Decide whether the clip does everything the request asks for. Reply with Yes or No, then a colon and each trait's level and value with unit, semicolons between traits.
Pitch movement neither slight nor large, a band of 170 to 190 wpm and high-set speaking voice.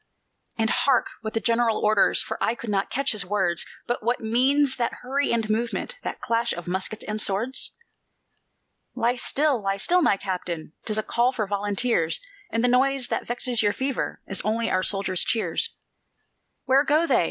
Yes: average, 3.6 semitones; average, 180 wpm; high, 230 Hz